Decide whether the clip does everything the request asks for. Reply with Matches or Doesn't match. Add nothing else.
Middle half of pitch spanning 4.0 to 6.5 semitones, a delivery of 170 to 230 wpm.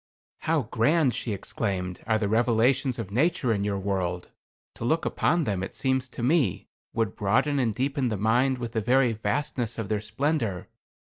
Matches